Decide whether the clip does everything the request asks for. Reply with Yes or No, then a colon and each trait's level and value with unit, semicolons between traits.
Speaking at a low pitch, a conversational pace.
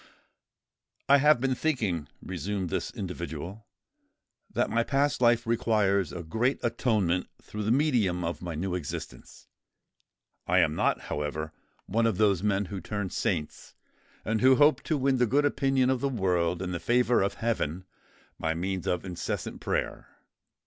Yes: low, 105 Hz; average, 155 wpm